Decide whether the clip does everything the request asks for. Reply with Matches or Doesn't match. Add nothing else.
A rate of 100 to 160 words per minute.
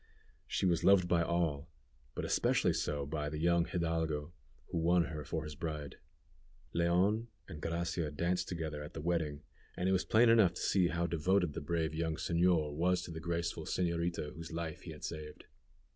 Doesn't match